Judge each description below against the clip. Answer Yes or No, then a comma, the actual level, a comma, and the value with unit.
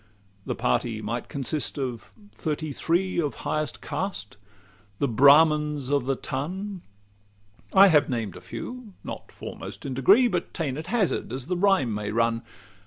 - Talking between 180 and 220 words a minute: No, average, 155 wpm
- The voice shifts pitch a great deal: Yes, wide, 6.5 semitones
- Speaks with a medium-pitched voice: Yes, medium, 145 Hz